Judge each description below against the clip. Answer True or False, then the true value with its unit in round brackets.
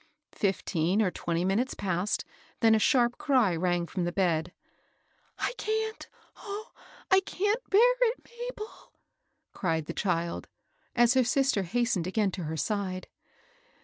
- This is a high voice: True (210 Hz)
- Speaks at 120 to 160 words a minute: True (155 wpm)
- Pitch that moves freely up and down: True (8.5 semitones)